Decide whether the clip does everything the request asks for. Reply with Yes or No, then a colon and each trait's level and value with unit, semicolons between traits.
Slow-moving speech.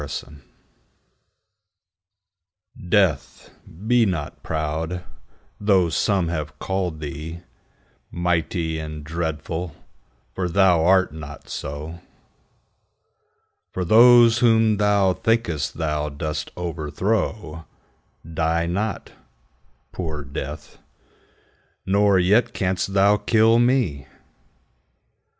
Yes: slow, 85 wpm